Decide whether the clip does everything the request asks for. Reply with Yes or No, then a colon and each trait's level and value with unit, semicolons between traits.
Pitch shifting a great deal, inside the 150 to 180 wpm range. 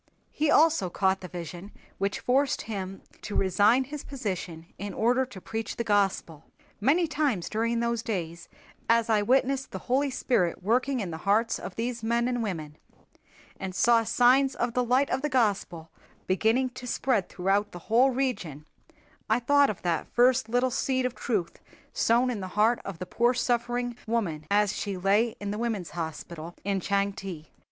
No: average, 4.7 semitones; average, 175 wpm